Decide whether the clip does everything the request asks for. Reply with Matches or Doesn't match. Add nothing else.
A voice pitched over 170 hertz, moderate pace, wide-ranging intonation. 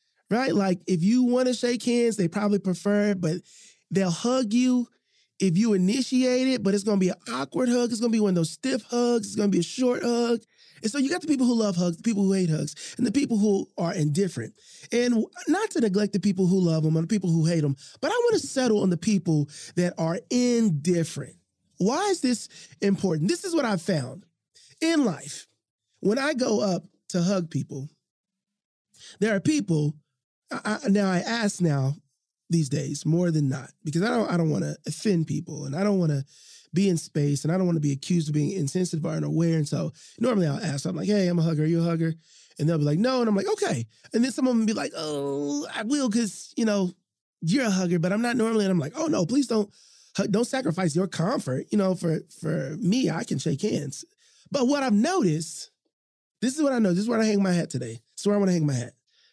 Doesn't match